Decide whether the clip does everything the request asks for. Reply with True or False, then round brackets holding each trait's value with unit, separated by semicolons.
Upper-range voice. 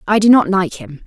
True (200 Hz)